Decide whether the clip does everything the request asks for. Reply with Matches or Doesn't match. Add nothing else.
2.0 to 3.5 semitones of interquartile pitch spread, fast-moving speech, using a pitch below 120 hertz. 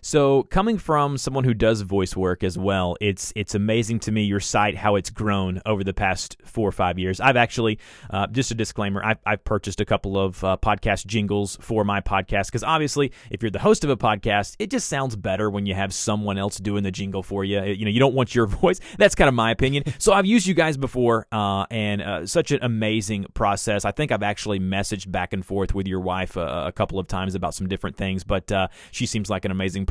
Matches